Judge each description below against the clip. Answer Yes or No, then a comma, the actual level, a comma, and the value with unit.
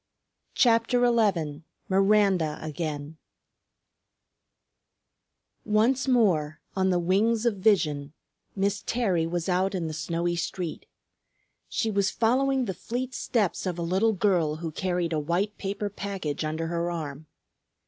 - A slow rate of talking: Yes, slow, 130 wpm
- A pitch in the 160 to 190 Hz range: Yes, medium, 185 Hz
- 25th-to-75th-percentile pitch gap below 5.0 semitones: Yes, average, 4.6 semitones